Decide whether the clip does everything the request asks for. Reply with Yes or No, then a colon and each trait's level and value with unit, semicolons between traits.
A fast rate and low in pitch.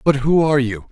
Yes: fast, 260 wpm; low, 130 Hz